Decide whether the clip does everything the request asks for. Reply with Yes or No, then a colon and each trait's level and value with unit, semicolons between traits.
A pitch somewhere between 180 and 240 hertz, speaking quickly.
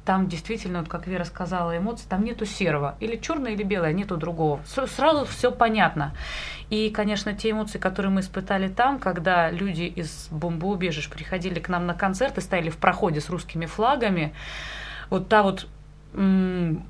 Yes: medium, 185 Hz; fast, 165 wpm